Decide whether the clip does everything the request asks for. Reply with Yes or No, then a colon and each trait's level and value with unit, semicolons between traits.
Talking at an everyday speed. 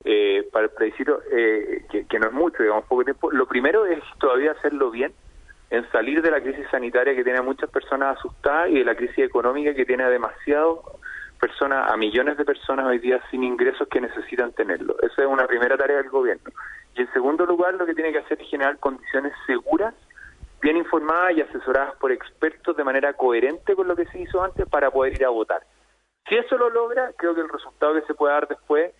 No: fast, 215 wpm